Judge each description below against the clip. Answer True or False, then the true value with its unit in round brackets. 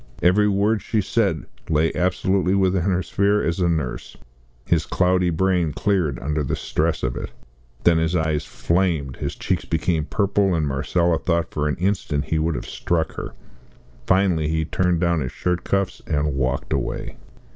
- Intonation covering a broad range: False (3.2 semitones)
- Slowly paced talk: False (170 wpm)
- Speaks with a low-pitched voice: True (85 Hz)